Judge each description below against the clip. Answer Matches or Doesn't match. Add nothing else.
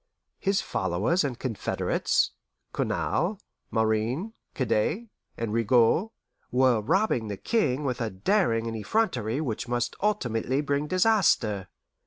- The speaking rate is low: Matches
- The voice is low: Matches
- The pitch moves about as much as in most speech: Doesn't match